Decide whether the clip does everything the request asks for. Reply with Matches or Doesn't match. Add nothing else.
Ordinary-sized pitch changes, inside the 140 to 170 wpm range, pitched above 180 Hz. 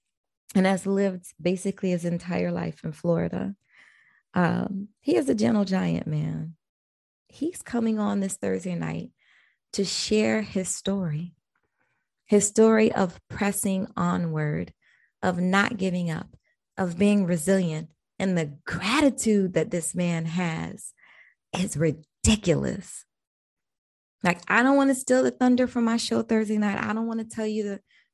Matches